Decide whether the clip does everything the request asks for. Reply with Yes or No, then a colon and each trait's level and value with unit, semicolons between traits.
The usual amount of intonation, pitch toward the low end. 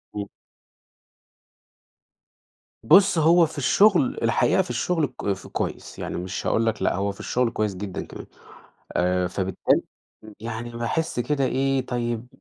No: wide, 6.4 semitones; low, 120 Hz